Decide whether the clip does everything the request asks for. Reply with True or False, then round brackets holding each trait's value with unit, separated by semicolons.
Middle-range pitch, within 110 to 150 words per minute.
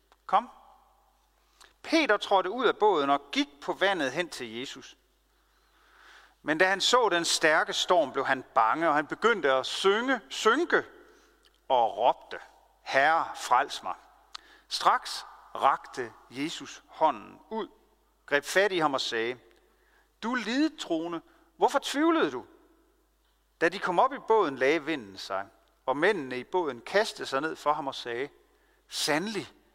False (250 Hz; 145 wpm)